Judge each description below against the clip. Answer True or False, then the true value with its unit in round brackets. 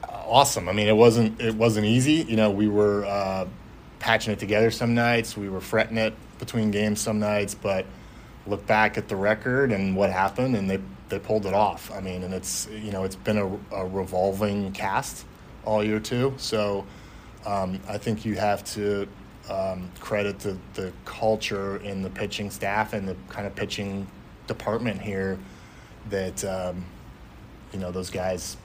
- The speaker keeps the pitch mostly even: True (2.1 semitones)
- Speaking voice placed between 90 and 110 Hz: True (105 Hz)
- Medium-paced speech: True (180 wpm)